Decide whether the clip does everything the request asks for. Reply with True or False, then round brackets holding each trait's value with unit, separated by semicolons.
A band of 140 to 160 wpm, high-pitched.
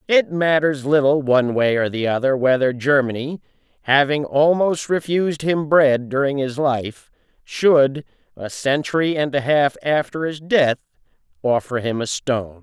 False (145 wpm; 140 Hz)